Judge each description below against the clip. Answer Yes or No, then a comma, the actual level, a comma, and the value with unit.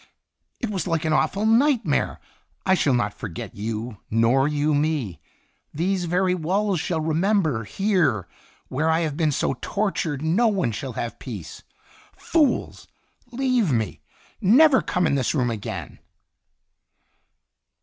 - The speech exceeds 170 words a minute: No, average, 140 wpm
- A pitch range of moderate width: No, wide, 7.5 semitones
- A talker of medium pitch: Yes, medium, 160 Hz